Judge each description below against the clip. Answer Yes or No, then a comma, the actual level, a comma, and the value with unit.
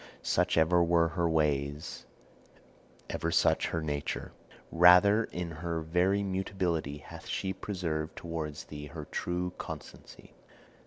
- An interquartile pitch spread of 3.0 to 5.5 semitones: No, narrow, 2.4 semitones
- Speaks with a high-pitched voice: No, very low, 85 Hz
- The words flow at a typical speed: No, slow, 120 wpm